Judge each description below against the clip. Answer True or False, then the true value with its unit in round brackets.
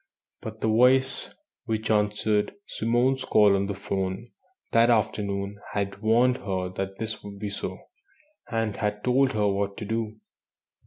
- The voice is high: False (105 Hz)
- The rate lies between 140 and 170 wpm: True (150 wpm)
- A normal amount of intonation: False (2.3 semitones)